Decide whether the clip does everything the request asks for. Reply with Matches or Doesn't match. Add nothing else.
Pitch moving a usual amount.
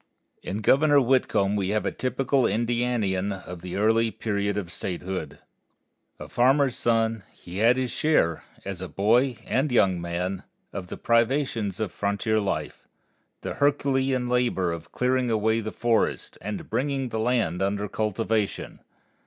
Matches